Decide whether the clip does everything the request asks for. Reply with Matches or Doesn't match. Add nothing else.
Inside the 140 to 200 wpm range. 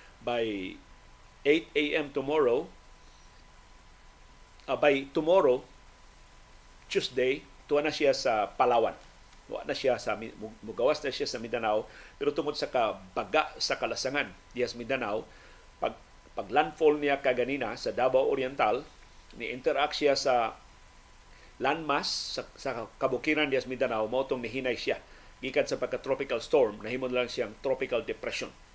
Doesn't match